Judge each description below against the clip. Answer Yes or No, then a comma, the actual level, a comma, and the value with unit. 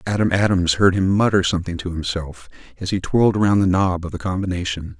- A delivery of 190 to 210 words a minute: Yes, fast, 205 wpm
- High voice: No, very low, 90 Hz